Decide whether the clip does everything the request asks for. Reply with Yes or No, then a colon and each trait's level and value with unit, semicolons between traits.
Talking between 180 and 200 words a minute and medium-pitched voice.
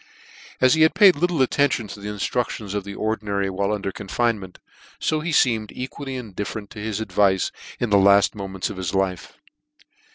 No: average, 185 wpm; low, 105 Hz